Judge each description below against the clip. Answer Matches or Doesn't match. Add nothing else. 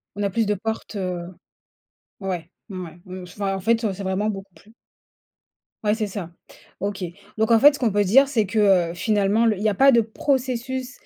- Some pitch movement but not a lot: Matches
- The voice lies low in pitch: Doesn't match